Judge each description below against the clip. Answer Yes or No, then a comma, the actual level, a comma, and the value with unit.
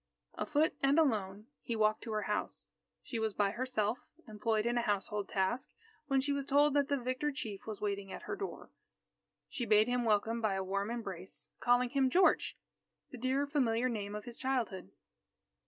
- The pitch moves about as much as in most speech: Yes, average, 4.1 semitones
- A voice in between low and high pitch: No, high, 230 Hz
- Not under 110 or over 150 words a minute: No, average, 185 wpm